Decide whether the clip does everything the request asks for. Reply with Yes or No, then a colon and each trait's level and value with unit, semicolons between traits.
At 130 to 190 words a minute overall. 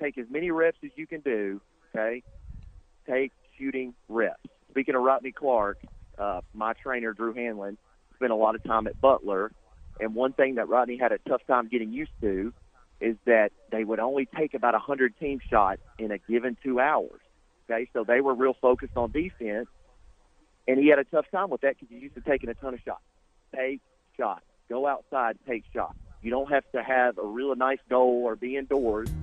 No: average, 200 wpm